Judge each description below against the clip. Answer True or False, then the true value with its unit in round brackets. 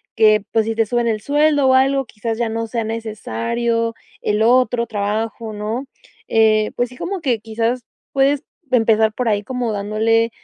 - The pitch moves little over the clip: True (2.2 semitones)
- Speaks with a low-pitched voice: False (225 Hz)